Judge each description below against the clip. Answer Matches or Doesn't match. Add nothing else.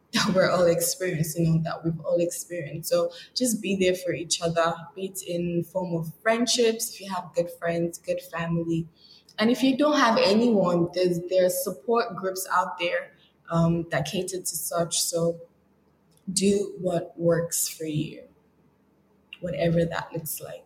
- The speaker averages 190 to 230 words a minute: Doesn't match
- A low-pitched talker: Doesn't match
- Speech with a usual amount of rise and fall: Doesn't match